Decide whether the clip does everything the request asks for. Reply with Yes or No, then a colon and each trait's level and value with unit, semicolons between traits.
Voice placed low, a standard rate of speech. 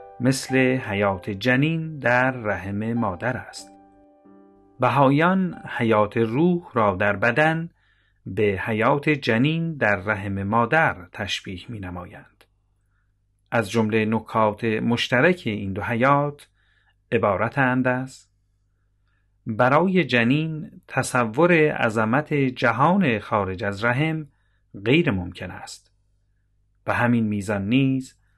No: low, 115 Hz; slow, 95 wpm